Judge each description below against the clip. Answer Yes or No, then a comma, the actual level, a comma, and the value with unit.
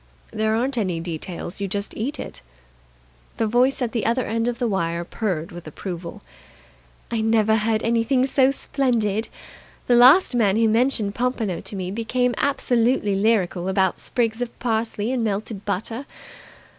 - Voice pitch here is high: Yes, high, 220 Hz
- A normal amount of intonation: Yes, average, 3.5 semitones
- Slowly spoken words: No, average, 155 wpm